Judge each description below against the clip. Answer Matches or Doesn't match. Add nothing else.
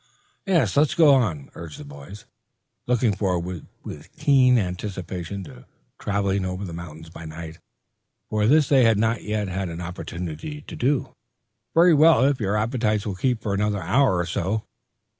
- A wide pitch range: Matches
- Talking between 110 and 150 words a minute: Doesn't match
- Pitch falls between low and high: Doesn't match